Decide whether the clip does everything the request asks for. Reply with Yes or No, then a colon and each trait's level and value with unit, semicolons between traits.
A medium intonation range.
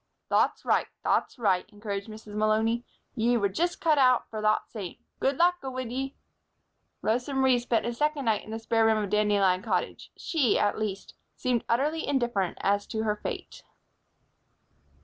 Yes: average, 3.6 semitones